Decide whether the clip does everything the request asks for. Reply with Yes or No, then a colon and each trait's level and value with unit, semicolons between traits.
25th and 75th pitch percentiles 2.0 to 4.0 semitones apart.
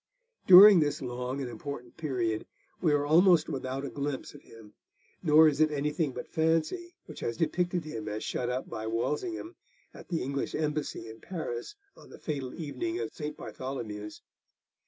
No: average, 4.6 semitones